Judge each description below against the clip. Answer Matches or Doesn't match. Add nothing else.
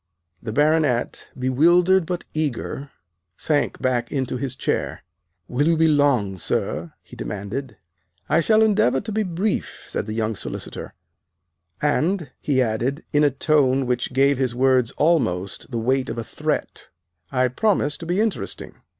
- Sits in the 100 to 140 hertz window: Matches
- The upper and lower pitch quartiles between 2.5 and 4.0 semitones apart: Doesn't match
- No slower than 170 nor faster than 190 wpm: Doesn't match